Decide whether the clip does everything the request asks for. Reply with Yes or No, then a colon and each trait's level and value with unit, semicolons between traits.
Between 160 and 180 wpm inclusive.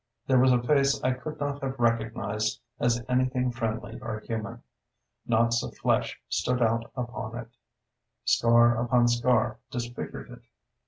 No: average, 145 wpm